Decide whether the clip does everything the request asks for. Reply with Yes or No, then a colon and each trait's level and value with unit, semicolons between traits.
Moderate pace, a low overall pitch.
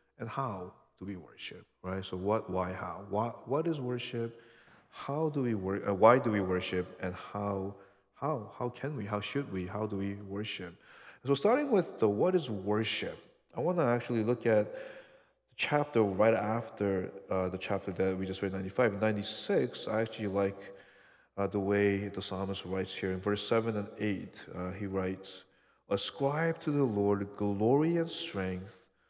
Yes: average, 180 wpm; low, 105 Hz